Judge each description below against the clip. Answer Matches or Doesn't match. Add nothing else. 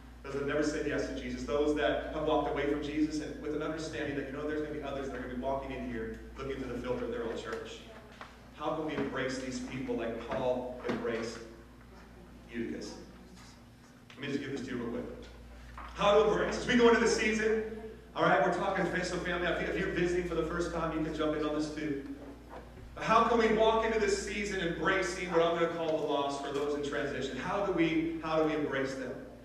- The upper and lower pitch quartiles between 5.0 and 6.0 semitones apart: Doesn't match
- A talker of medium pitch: Matches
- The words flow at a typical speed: Doesn't match